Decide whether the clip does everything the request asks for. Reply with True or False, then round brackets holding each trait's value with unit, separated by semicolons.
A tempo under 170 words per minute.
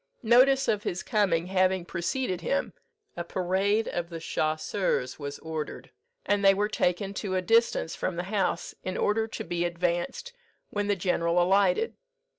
True (160 wpm)